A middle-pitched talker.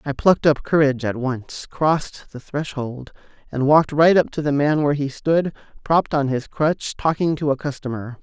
Yes: medium, 145 Hz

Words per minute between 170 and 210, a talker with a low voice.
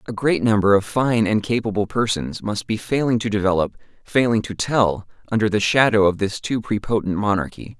Yes: average, 185 wpm; low, 105 Hz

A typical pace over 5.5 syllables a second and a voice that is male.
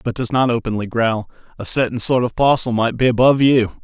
Yes: 5.8 syllables/s; male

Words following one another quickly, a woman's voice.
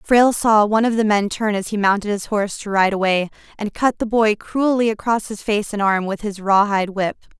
Yes: fast, 235 wpm; female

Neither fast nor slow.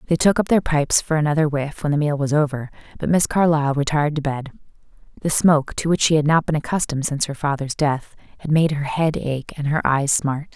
No: fast, 235 wpm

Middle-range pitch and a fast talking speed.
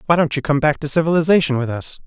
Yes: medium, 150 Hz; fast, 260 wpm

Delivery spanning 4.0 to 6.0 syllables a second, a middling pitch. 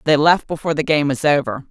No: 6.4 syllables/s; medium, 145 Hz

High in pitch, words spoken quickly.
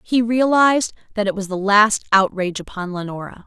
No: high, 210 Hz; average, 175 wpm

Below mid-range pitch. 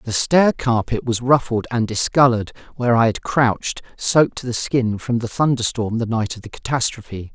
Yes: low, 120 Hz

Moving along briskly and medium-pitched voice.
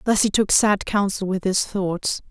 No: fast, 210 wpm; high, 195 Hz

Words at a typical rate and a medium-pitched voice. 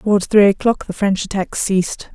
No: average, 195 wpm; high, 200 Hz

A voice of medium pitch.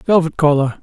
Yes: medium, 155 Hz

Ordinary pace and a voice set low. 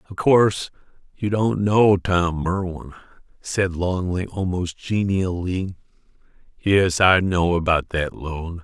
No: slow, 120 wpm; very low, 95 Hz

